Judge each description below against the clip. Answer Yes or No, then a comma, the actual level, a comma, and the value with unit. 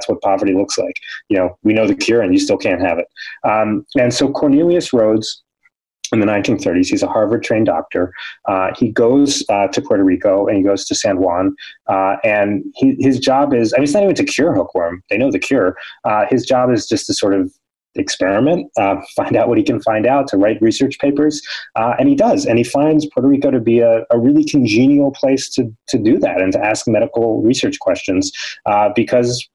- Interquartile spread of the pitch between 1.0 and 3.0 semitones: No, wide, 5.6 semitones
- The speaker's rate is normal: No, fast, 215 wpm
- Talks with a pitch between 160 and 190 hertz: No, low, 135 Hz